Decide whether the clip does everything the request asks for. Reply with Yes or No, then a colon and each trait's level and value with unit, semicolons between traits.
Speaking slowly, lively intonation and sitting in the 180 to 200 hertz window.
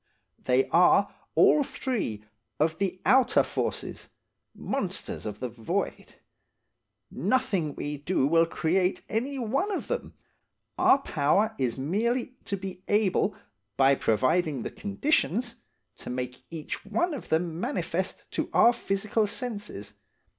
Yes: slow, 125 wpm; wide, 8.0 semitones; high, 190 Hz